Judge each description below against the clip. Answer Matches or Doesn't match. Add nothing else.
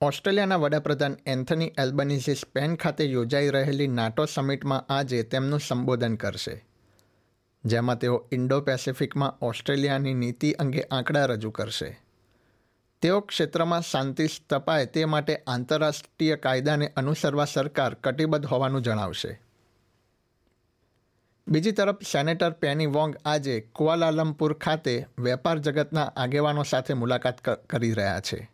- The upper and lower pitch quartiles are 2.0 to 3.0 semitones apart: Doesn't match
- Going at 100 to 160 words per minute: Matches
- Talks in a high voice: Doesn't match